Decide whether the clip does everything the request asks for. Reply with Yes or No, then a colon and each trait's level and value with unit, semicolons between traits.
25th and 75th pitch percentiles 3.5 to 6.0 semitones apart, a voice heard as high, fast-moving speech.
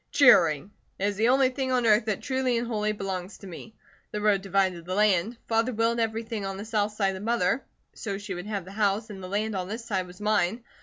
No: average, 2.9 semitones; high, 210 Hz; fast, 240 wpm